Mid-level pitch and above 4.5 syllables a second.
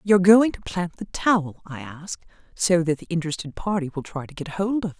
Yes: medium, 175 Hz; 6.1 syllables/s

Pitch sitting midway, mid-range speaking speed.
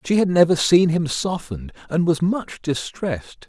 Yes: medium, 165 Hz; average, 170 wpm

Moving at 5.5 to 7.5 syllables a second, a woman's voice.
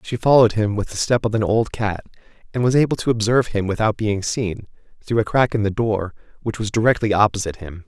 No: 6.3 syllables/s; male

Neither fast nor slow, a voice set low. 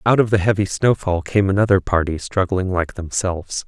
Yes: average, 180 wpm; very low, 95 Hz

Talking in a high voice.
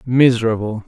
No: low, 115 Hz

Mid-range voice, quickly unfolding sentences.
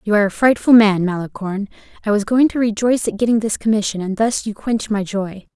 No: high, 215 Hz; fast, 225 wpm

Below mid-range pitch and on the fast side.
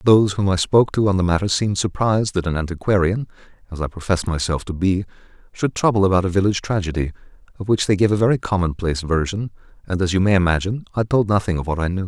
Yes: very low, 95 Hz; fast, 225 wpm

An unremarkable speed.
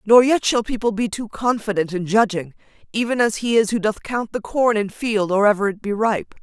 No: fast, 235 wpm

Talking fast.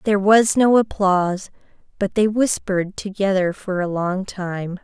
No: average, 150 wpm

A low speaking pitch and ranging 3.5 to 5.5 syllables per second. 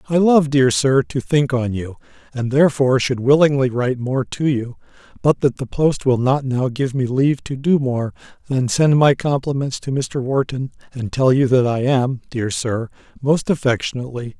Yes: low, 130 Hz; 4.9 syllables/s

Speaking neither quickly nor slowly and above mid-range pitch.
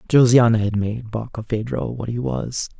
No: average, 150 wpm; low, 115 Hz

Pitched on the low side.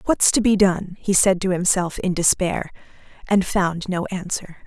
No: medium, 185 Hz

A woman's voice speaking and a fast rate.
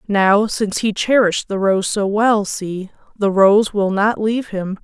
No: female; average, 185 wpm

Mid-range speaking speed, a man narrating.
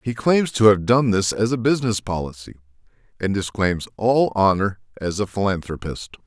Yes: average, 165 wpm; male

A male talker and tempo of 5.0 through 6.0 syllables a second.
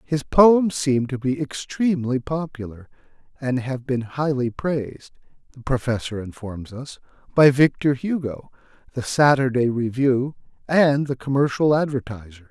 No: male; 4.6 syllables/s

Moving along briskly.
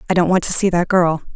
Yes: fast, 310 wpm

